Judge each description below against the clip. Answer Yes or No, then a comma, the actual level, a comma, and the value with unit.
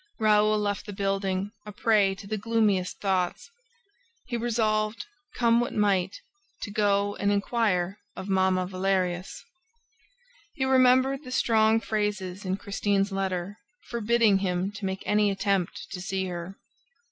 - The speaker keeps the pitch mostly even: Yes, narrow, 2.3 semitones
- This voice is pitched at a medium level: No, high, 200 Hz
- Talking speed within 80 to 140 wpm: Yes, slow, 135 wpm